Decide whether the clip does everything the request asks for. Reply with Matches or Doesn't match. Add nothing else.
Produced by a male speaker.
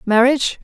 Doesn't match